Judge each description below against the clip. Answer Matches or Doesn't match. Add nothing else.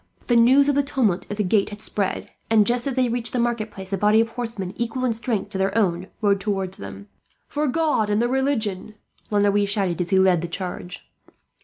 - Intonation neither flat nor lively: Matches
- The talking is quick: Matches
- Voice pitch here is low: Doesn't match